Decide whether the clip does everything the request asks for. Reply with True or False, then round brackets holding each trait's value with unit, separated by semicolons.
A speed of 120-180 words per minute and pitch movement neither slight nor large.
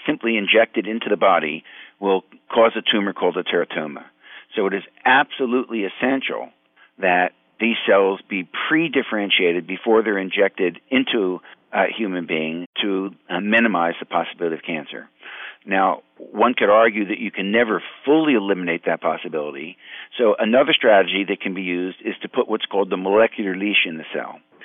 True (160 wpm; 3.4 semitones)